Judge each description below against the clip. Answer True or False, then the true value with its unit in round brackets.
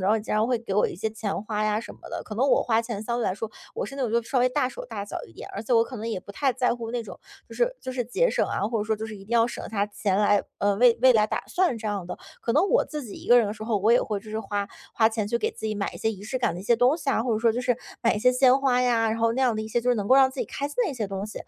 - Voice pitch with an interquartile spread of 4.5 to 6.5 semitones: False (2.9 semitones)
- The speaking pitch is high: True (225 Hz)